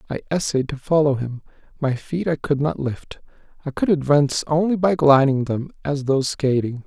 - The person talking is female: No, male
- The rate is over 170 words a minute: Yes, average, 185 wpm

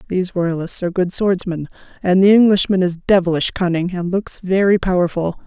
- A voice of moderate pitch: Yes, medium, 180 Hz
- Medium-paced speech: Yes, average, 165 wpm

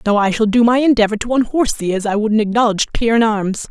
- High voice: Yes, high, 220 Hz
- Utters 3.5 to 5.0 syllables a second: No, 6.8 syllables/s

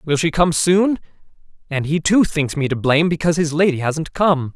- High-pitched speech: No, medium, 160 Hz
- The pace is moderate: No, fast, 210 wpm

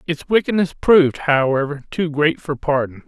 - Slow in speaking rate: No, average, 155 wpm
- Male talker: Yes, male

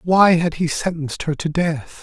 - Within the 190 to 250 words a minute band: Yes, fast, 205 wpm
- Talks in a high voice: No, medium, 165 Hz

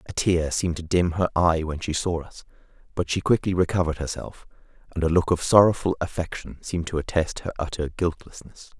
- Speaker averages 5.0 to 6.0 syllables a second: Yes, 5.9 syllables/s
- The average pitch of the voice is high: No, very low, 85 Hz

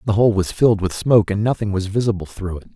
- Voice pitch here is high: No, low, 105 Hz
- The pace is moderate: No, fast, 260 wpm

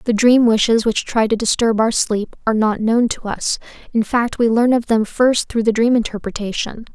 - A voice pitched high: Yes, high, 225 Hz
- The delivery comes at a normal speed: No, fast, 215 wpm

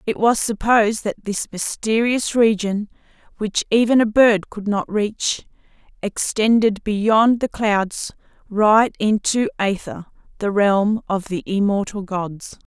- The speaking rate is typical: No, slow, 125 wpm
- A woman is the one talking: Yes, female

